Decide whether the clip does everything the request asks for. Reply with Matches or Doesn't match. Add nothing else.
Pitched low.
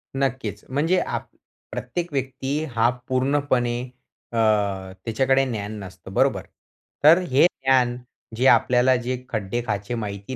Matches